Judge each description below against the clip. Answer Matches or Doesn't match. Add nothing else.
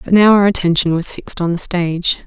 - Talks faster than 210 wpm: Matches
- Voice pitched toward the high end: Doesn't match